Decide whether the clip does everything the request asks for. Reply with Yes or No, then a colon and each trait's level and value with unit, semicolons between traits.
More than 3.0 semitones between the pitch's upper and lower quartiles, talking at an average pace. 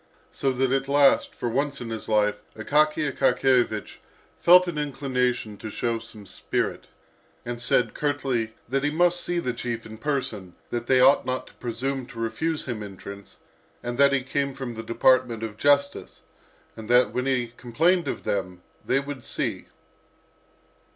Yes: average, 3.7 semitones; average, 165 wpm